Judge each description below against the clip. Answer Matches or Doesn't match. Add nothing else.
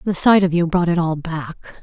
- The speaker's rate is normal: Doesn't match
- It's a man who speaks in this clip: Doesn't match